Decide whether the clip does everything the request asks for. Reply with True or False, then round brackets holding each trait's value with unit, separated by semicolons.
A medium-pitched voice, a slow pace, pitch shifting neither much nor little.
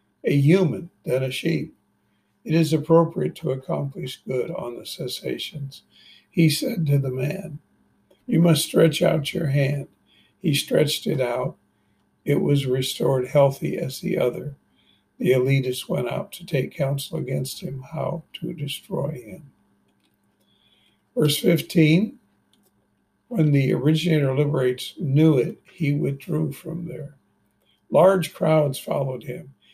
True (150 Hz; 130 wpm; 3.8 semitones)